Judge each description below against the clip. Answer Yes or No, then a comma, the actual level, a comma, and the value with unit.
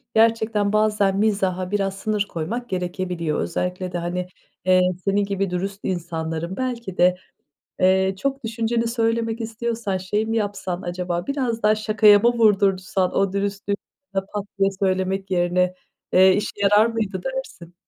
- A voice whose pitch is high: Yes, high, 195 Hz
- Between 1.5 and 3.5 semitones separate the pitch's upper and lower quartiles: Yes, average, 3.1 semitones